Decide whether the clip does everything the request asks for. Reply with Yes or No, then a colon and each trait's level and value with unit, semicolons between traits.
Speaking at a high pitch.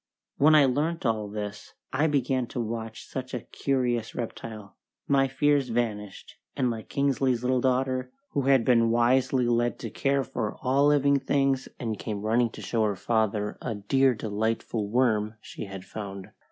No: low, 120 Hz